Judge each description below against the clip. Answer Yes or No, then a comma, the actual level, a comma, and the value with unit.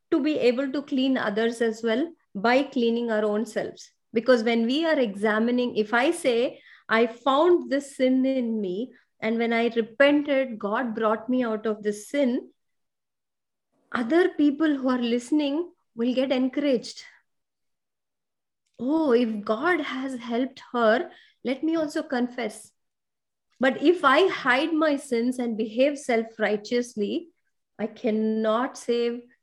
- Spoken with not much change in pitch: No, average, 3.8 semitones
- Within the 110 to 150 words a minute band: Yes, average, 140 wpm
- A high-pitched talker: Yes, high, 245 Hz